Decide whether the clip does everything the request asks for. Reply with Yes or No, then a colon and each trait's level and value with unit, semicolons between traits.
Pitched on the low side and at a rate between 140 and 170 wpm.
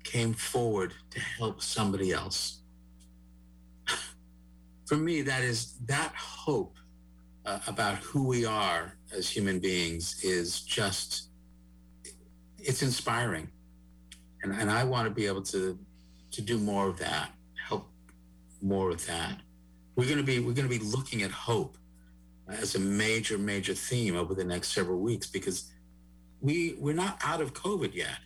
Yes: very low, 90 Hz; average, 150 wpm